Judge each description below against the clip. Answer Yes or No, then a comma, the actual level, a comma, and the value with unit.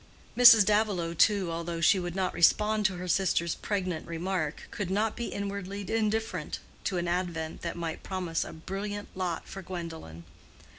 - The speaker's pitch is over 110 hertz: Yes, medium, 185 Hz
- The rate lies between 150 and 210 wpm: Yes, average, 160 wpm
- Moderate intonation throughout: Yes, average, 3.2 semitones